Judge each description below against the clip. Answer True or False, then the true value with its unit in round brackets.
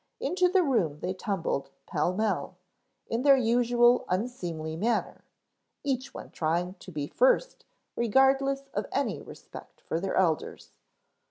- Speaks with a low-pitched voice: False (225 Hz)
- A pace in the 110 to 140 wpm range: True (135 wpm)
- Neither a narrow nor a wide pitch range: False (7.1 semitones)